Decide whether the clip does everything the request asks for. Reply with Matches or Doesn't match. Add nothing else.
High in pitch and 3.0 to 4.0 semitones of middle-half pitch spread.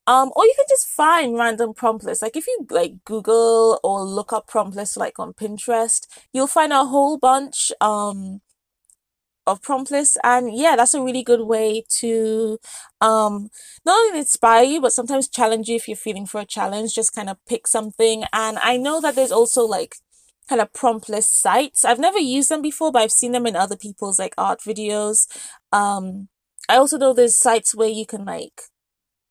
Matches